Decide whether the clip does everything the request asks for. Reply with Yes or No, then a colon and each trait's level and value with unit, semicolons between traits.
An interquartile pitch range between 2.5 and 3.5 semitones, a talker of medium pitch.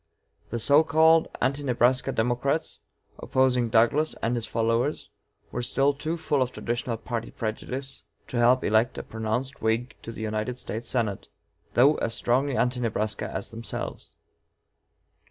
No: average, 3.0 semitones; low, 120 Hz